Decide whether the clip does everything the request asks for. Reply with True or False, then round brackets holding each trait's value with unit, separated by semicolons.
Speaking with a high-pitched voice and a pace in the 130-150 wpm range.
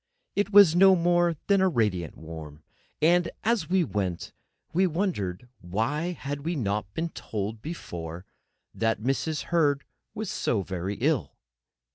False (140 Hz; 135 wpm)